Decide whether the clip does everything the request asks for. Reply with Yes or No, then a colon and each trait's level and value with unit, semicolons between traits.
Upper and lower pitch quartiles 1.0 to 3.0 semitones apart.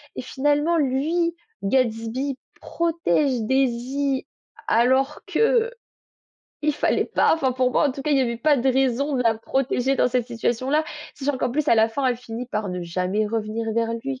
No: average, 3.5 semitones